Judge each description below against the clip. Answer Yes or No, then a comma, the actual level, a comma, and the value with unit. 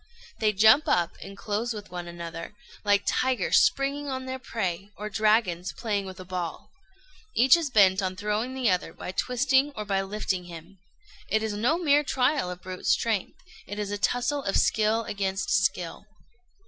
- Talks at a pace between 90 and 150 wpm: No, average, 175 wpm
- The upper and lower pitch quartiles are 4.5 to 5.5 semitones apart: Yes, average, 4.8 semitones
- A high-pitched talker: Yes, high, 210 Hz